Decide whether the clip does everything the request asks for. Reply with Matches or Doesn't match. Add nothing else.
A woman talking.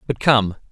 Doesn't match